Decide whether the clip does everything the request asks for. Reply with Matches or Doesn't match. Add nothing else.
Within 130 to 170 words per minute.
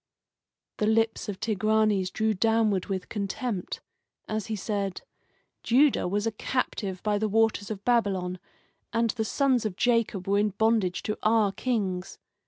Matches